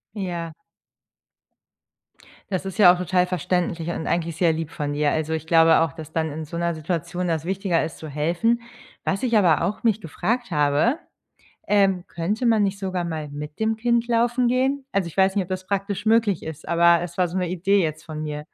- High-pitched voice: No, medium, 175 Hz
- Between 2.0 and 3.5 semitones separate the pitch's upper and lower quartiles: No, average, 3.9 semitones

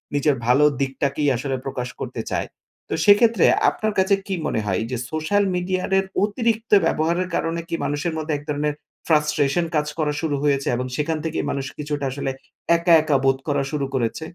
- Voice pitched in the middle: Yes, medium, 150 Hz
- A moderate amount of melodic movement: Yes, average, 3.9 semitones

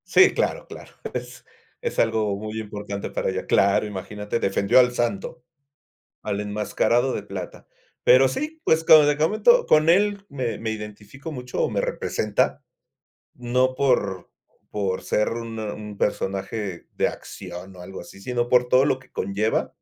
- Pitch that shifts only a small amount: No, average, 4.5 semitones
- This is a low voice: Yes, low, 110 Hz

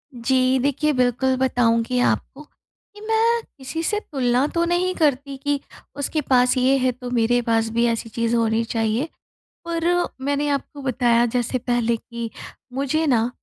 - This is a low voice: No, very high, 255 Hz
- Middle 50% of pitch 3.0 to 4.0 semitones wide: Yes, average, 3.3 semitones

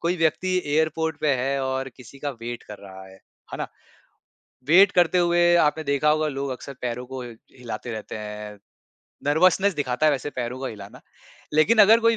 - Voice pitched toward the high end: No, medium, 140 Hz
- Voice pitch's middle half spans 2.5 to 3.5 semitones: No, average, 4.9 semitones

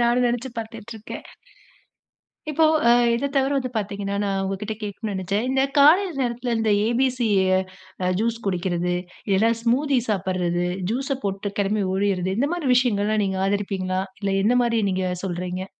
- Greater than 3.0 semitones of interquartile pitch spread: Yes, average, 4.0 semitones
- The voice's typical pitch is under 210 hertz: No, high, 215 Hz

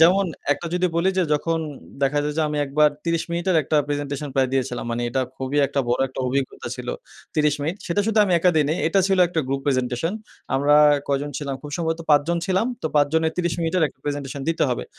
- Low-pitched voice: No, medium, 150 Hz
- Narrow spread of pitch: No, average, 3.4 semitones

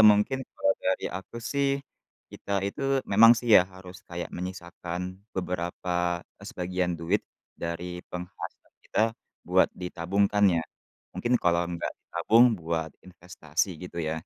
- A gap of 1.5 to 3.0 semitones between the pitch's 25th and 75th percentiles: Yes, narrow, 2.6 semitones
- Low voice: Yes, very low, 90 Hz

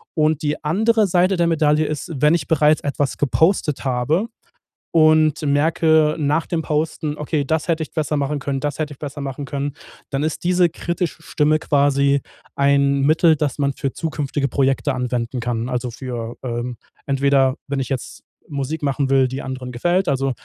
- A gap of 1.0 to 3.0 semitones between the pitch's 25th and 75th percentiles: Yes, narrow, 2.6 semitones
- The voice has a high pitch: No, medium, 145 Hz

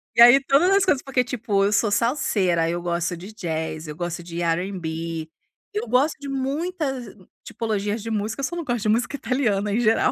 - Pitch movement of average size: No, wide, 6.9 semitones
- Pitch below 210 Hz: No, high, 215 Hz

